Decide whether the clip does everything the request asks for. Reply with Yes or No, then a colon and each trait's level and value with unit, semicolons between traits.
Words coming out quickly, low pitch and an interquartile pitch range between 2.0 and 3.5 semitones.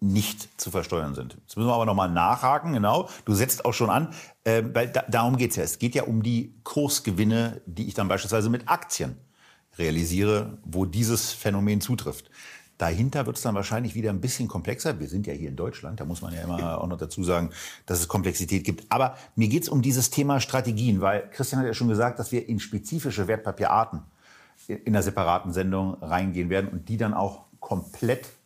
No: fast, 205 wpm; low, 105 Hz; average, 4.2 semitones